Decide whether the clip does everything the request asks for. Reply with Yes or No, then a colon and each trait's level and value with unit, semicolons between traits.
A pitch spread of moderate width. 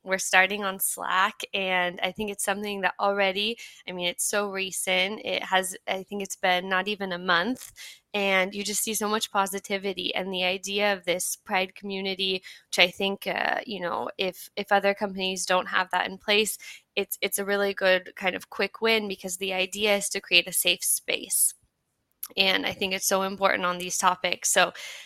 No: narrow, 1.5 semitones